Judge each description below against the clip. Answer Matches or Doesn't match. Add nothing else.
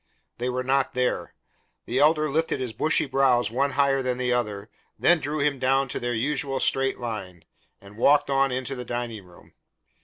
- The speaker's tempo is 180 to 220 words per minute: Matches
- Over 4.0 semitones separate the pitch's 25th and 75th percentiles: Doesn't match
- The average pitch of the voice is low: Matches